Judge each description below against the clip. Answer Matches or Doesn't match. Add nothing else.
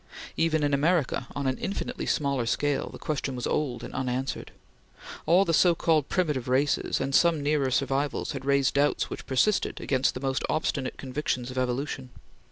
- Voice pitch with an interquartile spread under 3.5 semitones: Matches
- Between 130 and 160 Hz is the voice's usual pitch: Matches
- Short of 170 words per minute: Doesn't match